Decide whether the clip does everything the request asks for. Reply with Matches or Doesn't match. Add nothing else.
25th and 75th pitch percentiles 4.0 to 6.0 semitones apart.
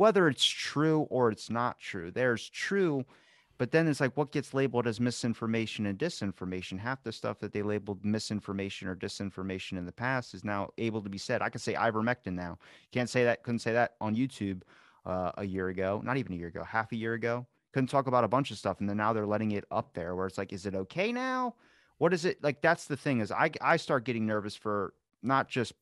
Matches